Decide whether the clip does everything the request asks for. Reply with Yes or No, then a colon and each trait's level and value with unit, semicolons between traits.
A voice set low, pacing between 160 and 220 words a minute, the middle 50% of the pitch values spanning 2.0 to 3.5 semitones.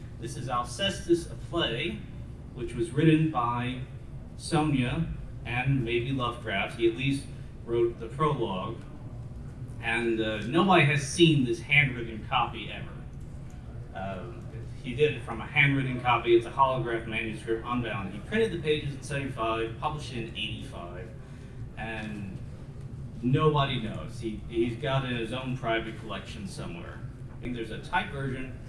No: low, 125 Hz; average, 145 wpm; average, 3.0 semitones